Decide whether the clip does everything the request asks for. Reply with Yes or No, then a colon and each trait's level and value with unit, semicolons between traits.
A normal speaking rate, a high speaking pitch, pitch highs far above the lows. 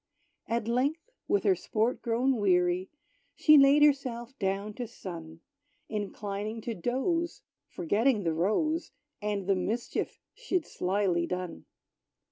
No: slow, 120 wpm; high, 220 Hz; wide, 6.0 semitones